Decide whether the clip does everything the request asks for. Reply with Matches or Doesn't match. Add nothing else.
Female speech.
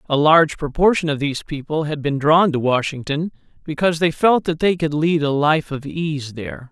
Doesn't match